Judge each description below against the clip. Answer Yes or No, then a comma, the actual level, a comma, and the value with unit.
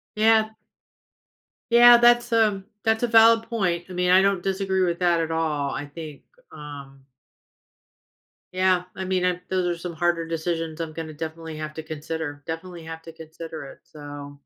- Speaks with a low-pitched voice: No, medium, 170 Hz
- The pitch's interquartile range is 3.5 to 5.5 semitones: No, average, 3.1 semitones